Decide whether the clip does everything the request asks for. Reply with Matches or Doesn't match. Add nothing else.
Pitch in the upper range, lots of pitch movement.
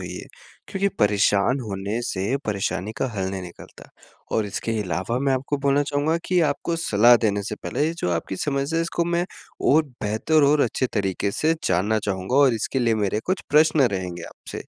Doesn't match